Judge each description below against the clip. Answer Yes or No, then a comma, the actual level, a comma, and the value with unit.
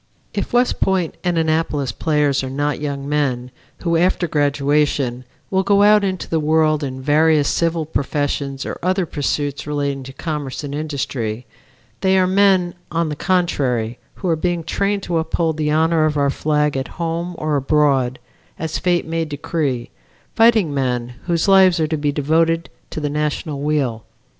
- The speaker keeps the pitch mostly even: No, average, 3.1 semitones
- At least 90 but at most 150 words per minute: No, average, 165 wpm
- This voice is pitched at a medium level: Yes, medium, 150 Hz